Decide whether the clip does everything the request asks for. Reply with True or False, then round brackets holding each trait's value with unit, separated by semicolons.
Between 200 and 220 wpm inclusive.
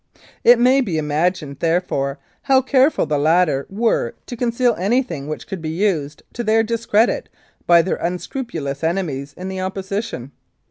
False (150 wpm)